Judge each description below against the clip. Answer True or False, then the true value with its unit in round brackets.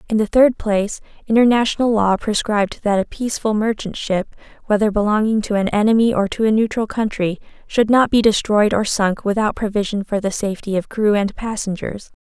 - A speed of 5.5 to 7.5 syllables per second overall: True (5.6 syllables/s)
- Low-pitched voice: False (210 Hz)